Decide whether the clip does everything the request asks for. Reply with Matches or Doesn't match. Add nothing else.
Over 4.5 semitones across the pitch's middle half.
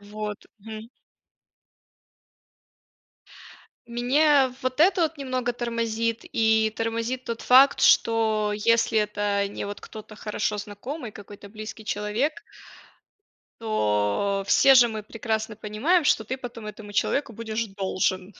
Doesn't match